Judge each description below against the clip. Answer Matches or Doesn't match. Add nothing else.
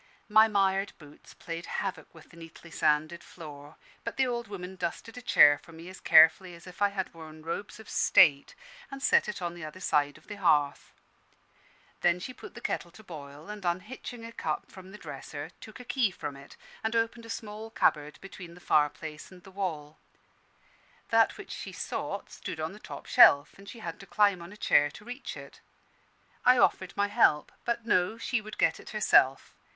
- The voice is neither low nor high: Matches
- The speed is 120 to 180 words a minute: Doesn't match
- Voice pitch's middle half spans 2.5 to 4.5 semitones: Doesn't match